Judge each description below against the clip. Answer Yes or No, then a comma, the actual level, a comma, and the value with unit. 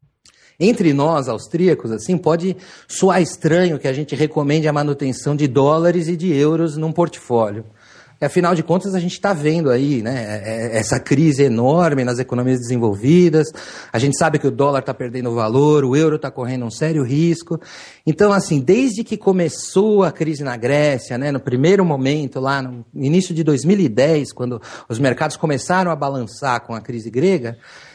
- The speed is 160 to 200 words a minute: Yes, average, 170 wpm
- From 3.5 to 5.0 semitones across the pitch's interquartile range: Yes, average, 4.7 semitones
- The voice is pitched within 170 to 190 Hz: No, medium, 150 Hz